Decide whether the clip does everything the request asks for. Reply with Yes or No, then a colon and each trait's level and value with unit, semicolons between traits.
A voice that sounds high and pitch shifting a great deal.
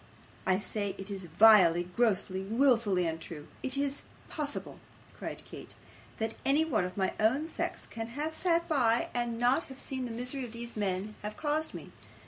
Yes: high, 230 Hz; wide, 5.9 semitones